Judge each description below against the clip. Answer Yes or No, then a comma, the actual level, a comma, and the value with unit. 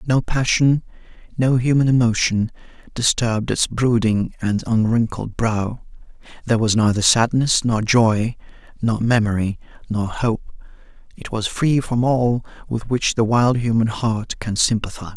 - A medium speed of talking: No, slow, 130 wpm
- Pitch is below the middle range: Yes, low, 115 Hz